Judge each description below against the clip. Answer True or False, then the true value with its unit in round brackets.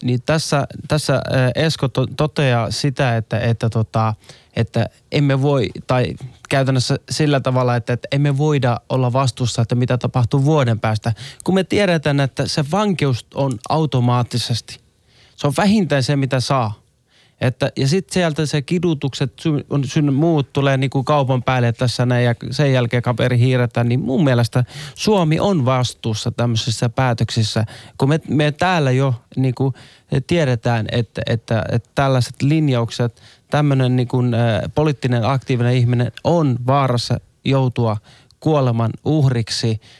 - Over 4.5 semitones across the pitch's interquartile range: False (3.1 semitones)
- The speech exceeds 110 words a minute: True (135 wpm)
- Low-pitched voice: True (130 Hz)